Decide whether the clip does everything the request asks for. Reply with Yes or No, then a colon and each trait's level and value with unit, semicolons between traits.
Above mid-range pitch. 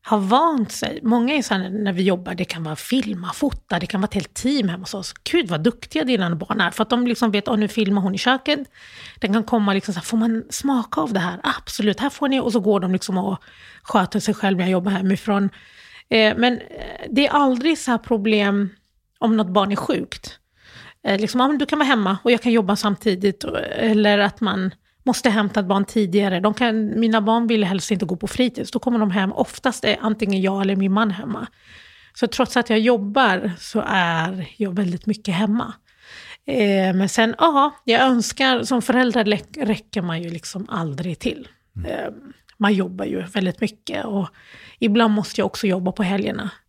Yes: high, 215 Hz